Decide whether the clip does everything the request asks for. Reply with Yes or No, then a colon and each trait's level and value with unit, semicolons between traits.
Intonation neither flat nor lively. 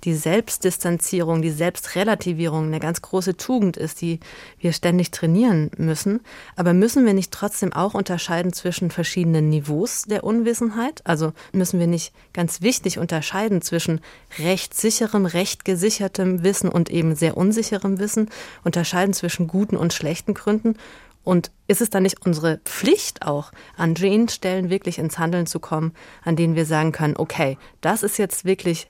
Yes: average, 3.5 semitones